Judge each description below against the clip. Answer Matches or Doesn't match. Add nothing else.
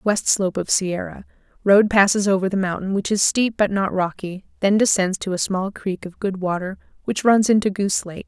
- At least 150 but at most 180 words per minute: Doesn't match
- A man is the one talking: Doesn't match